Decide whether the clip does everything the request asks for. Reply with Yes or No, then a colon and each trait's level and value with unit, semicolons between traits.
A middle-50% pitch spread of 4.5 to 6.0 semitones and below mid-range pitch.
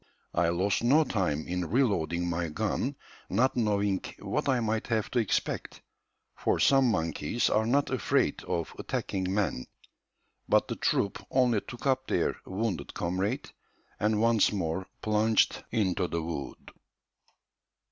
Yes: average, 5.1 semitones; low, 105 Hz